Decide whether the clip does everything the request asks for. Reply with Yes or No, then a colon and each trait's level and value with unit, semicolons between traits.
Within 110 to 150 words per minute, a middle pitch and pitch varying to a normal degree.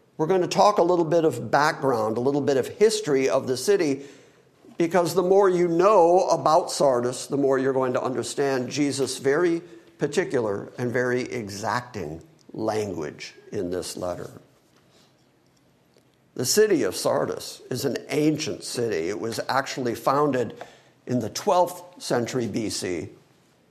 No: average, 145 wpm; medium, 145 Hz; wide, 5.9 semitones